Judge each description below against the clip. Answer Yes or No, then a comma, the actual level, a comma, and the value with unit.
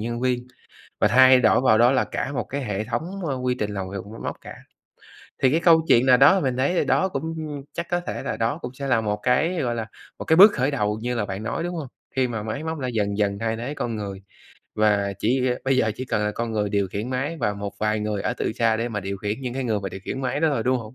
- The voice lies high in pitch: No, low, 120 Hz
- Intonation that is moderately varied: Yes, average, 4.2 semitones